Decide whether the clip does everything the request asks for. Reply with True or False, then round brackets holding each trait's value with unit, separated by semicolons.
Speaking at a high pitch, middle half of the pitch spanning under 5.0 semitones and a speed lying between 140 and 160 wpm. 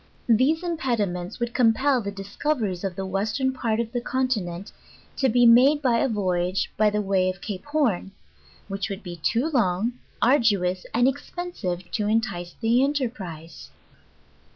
False (220 Hz; 5.3 semitones; 155 wpm)